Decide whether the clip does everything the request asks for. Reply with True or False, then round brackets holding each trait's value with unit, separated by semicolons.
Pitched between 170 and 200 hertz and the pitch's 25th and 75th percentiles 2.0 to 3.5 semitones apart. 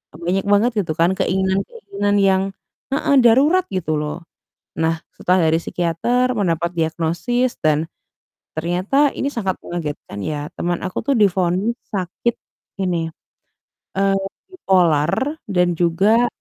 False (185 Hz; 4.9 semitones)